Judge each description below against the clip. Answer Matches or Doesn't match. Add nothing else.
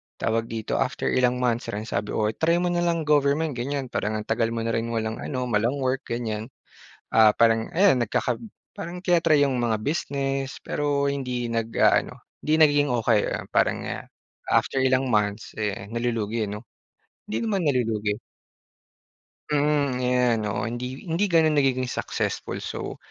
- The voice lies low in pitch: Matches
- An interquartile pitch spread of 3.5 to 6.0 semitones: Matches